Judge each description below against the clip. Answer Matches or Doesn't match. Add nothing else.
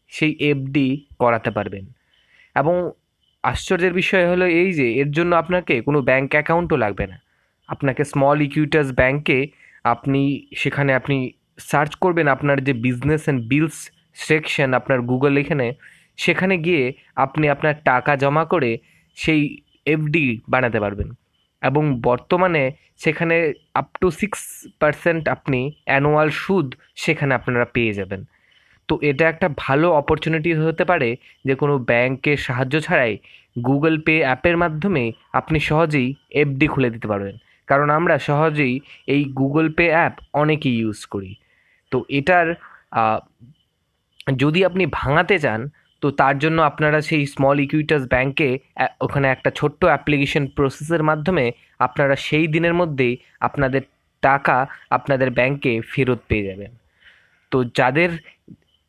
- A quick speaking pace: Matches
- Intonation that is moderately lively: Matches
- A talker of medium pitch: Matches